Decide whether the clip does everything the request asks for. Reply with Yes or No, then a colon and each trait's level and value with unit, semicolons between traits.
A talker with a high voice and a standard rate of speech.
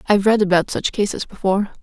Yes: high, 200 Hz; average, 195 wpm